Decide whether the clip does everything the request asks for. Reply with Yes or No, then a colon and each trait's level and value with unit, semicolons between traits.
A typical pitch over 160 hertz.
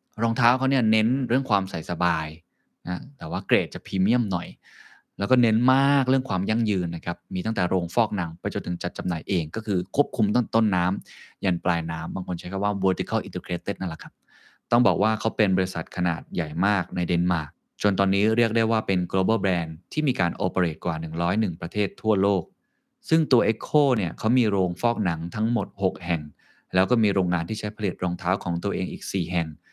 No: very low, 95 Hz